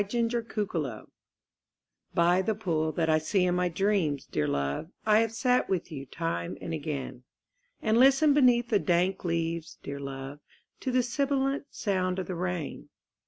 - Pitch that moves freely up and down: Yes, wide, 6.3 semitones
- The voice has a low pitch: No, medium, 180 Hz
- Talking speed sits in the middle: Yes, average, 165 wpm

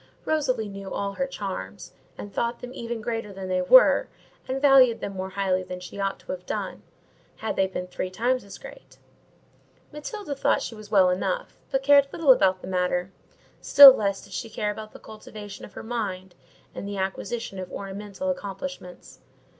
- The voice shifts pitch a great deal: No, average, 4.9 semitones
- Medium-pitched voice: No, high, 205 Hz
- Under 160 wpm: No, average, 185 wpm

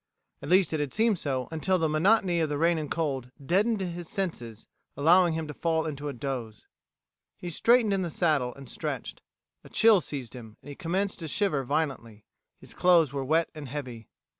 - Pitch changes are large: No, average, 4.7 semitones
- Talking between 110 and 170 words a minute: No, average, 195 wpm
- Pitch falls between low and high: Yes, medium, 160 Hz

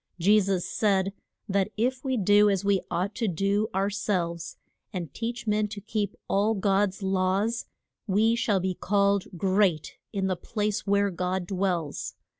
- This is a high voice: Yes, high, 200 Hz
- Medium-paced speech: Yes, average, 160 wpm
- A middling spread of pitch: No, narrow, 1.9 semitones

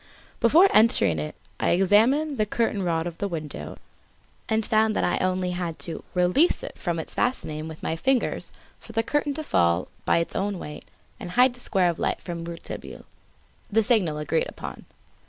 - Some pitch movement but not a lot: No, wide, 5.8 semitones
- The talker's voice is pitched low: No, high, 190 Hz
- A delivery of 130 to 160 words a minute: No, average, 185 wpm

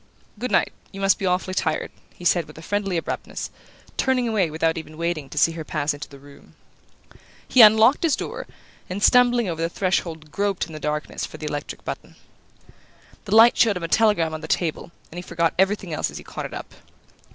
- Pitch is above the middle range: No, medium, 175 Hz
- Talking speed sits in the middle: No, fast, 210 wpm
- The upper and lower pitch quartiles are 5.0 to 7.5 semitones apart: No, average, 4.6 semitones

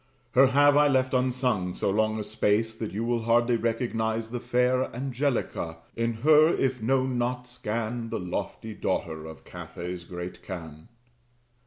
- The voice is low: Yes, low, 115 Hz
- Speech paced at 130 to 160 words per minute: Yes, average, 155 wpm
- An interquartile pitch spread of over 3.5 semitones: No, average, 3.2 semitones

